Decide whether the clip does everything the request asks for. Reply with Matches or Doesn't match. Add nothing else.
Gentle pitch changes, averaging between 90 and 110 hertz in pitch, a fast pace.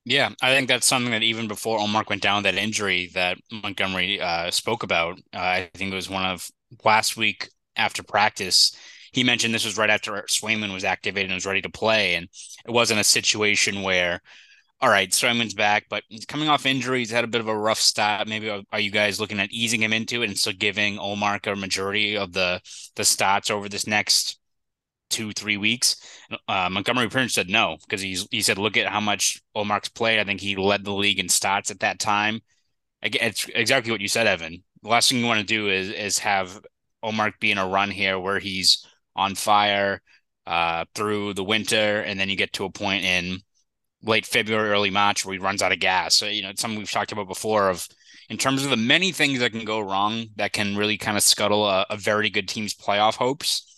Matches